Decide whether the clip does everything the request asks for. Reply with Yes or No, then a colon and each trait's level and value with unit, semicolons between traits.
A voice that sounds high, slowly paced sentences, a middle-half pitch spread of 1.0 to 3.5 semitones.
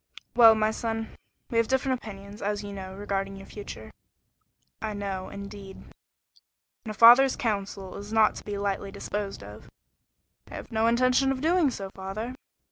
No: high, 210 Hz; average, 165 wpm; average, 2.7 semitones